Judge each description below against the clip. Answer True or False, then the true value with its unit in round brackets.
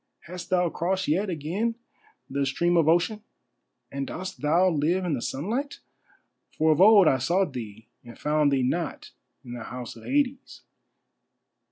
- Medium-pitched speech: True (165 Hz)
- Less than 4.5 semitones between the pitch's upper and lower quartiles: False (5.3 semitones)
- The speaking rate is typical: True (160 wpm)